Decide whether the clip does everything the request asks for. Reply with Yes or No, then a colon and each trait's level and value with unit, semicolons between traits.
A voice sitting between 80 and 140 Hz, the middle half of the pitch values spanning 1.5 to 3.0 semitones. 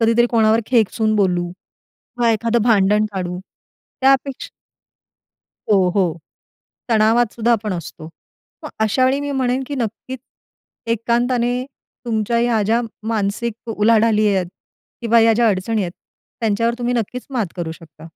No: high, 225 Hz; average, 2.7 semitones